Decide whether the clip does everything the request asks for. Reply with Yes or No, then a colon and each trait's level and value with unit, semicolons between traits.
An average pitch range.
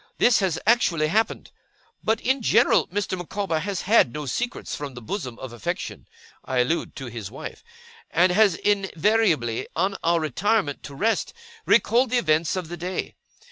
No: wide, 6.2 semitones